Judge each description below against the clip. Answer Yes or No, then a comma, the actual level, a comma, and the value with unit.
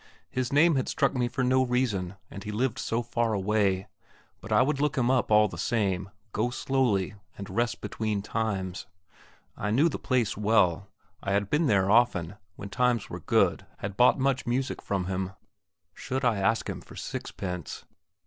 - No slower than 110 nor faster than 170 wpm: No, average, 180 wpm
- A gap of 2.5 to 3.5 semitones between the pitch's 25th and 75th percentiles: No, average, 4.3 semitones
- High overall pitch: No, low, 110 Hz